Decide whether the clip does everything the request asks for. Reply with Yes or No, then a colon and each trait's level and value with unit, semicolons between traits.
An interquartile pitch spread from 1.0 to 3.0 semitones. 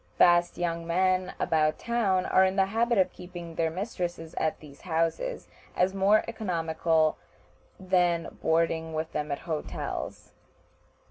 Yes: narrow, 2.6 semitones